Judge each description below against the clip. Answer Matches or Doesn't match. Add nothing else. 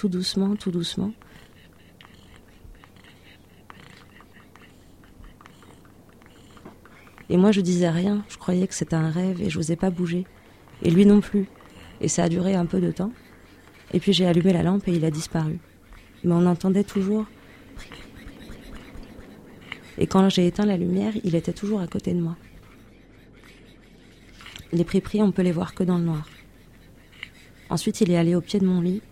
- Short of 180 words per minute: Matches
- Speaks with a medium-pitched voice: Matches